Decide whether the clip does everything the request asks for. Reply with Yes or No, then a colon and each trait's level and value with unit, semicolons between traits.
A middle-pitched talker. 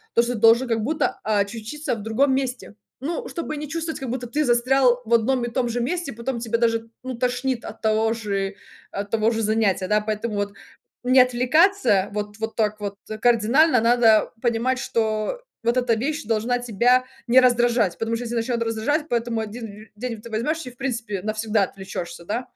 No: high, 235 Hz